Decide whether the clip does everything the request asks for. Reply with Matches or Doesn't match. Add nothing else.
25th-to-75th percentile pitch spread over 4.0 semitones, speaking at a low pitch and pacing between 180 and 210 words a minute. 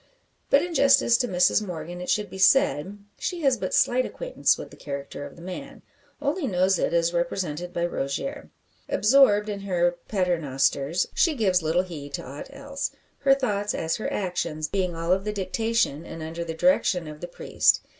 Doesn't match